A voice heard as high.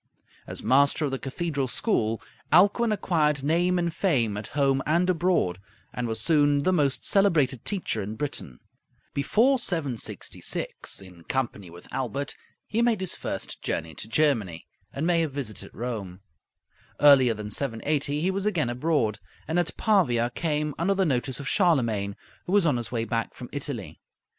No: medium, 140 Hz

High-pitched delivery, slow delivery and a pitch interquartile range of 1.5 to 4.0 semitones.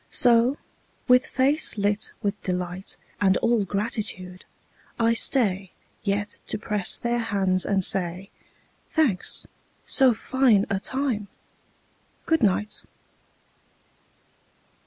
Yes: high, 210 Hz; slow, 100 wpm; average, 3.7 semitones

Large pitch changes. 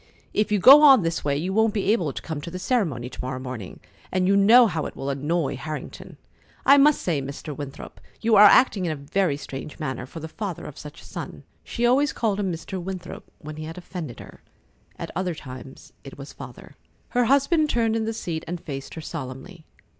Yes: wide, 6.9 semitones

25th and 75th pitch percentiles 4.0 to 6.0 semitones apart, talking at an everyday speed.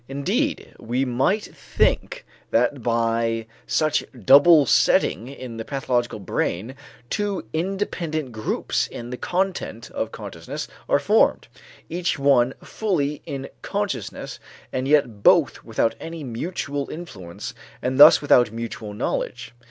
No: average, 5.1 semitones; slow, 120 wpm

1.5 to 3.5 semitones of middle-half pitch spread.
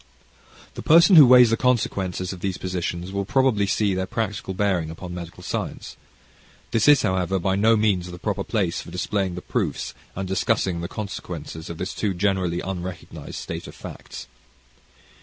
Yes: average, 2.9 semitones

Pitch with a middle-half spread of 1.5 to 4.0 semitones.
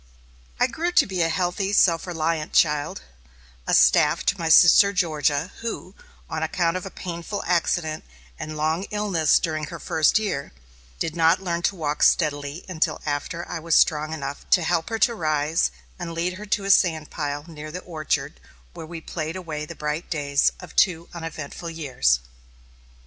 Yes: average, 2.7 semitones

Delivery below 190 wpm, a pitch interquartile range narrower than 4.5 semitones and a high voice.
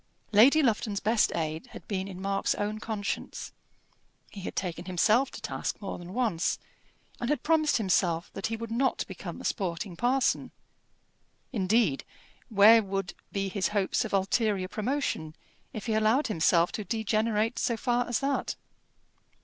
Yes: average, 155 wpm; average, 3.5 semitones; high, 210 Hz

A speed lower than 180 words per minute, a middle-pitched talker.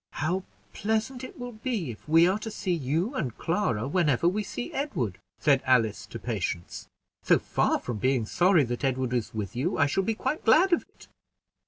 No: average, 195 wpm; medium, 155 Hz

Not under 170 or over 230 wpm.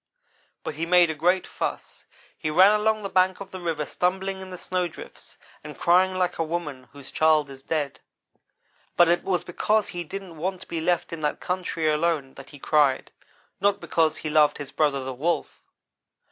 Yes: average, 190 wpm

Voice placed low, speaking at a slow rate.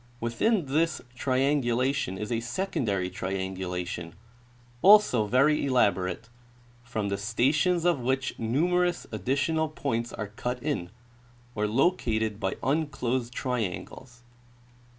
Yes: low, 125 Hz; slow, 110 wpm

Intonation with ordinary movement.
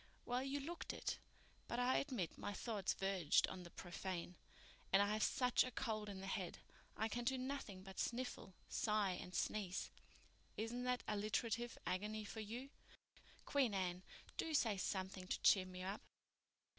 Yes: average, 4.6 semitones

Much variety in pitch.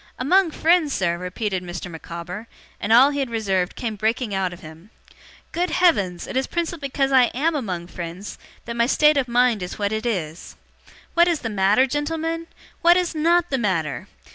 Yes: wide, 8.3 semitones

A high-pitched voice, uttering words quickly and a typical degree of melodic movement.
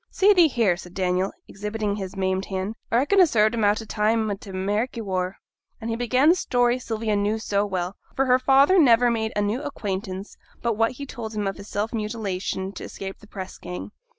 Yes: high, 215 Hz; fast, 215 wpm; average, 3.5 semitones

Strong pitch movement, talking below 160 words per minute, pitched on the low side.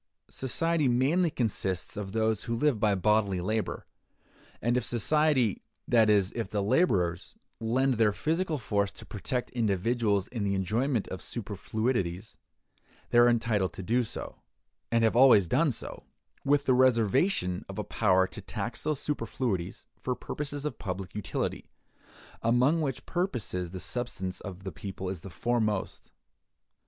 No: average, 4.7 semitones; average, 150 wpm; low, 115 Hz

